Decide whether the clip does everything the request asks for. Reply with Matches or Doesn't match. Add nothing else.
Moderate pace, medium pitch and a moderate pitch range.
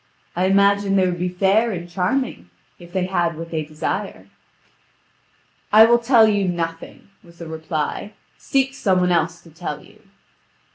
Matches